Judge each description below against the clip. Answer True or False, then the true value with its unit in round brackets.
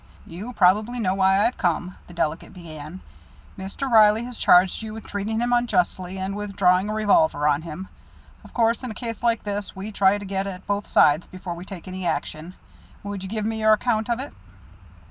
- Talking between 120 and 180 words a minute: False (205 wpm)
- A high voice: True (200 Hz)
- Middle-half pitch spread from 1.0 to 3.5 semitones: True (3.2 semitones)